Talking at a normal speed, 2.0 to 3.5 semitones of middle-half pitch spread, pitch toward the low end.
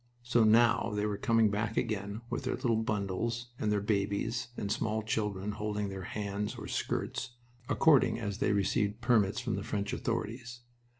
Yes: average, 175 wpm; narrow, 2.4 semitones; low, 110 Hz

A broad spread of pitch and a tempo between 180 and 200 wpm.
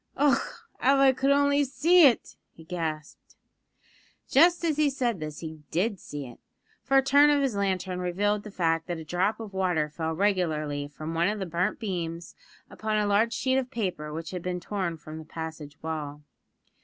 Yes: wide, 7.2 semitones; average, 190 wpm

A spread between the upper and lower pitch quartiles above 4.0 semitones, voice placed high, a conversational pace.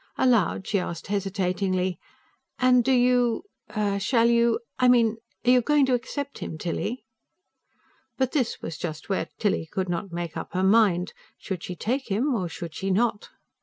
Yes: average, 5.2 semitones; high, 210 Hz; average, 165 wpm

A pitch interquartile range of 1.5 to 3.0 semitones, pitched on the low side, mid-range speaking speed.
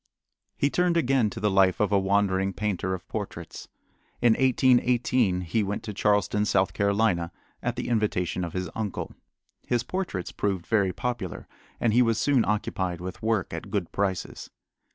No: average, 4.1 semitones; low, 105 Hz; average, 165 wpm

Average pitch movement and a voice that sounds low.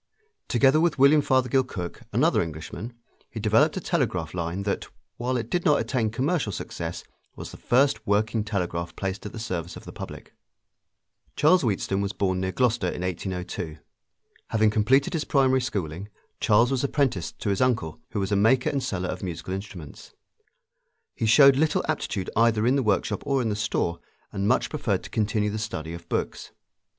No: wide, 5.8 semitones; low, 110 Hz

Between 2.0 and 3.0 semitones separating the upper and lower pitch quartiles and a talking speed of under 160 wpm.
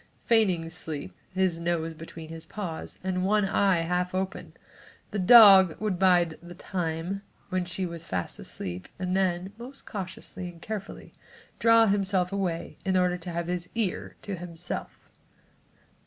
Yes: narrow, 2.4 semitones; average, 150 wpm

